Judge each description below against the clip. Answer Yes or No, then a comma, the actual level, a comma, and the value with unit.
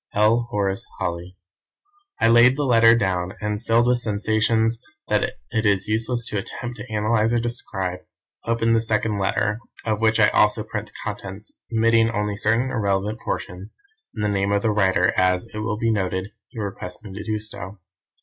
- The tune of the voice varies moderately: No, narrow, 2.3 semitones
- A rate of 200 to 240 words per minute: No, average, 180 wpm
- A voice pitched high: No, low, 105 Hz